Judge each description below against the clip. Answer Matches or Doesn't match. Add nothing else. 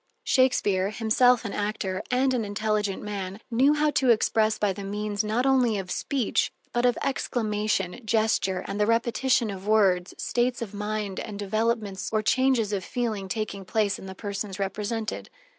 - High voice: Matches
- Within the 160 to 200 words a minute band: Matches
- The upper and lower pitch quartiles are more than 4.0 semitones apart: Doesn't match